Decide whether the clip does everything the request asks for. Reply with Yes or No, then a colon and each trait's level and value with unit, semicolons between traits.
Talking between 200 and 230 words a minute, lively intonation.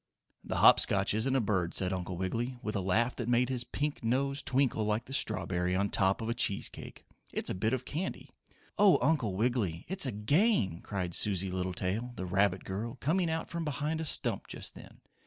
Yes: fast, 205 wpm; wide, 6.1 semitones